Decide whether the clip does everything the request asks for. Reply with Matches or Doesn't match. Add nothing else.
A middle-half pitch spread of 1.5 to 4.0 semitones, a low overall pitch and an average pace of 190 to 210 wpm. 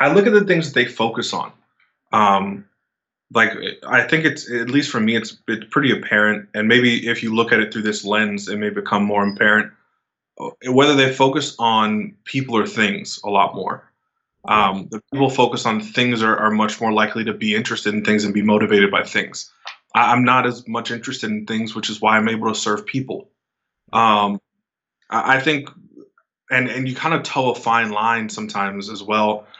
Matches